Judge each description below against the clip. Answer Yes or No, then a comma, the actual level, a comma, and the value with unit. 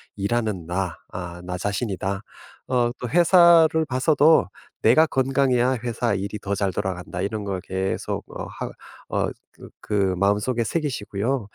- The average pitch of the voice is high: No, low, 105 Hz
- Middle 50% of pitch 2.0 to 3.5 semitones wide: No, average, 5.1 semitones